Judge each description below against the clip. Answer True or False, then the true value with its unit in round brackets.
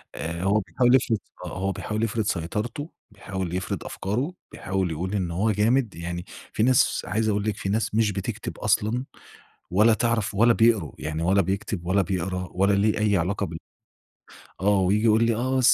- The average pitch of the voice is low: True (100 Hz)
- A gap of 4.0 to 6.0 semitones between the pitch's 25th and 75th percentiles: False (3.2 semitones)